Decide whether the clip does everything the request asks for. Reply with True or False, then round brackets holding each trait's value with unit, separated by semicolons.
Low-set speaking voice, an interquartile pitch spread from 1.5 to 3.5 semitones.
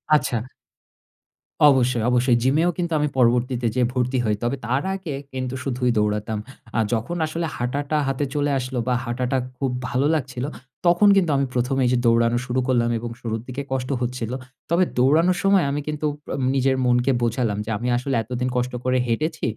True (125 Hz; 2.9 semitones)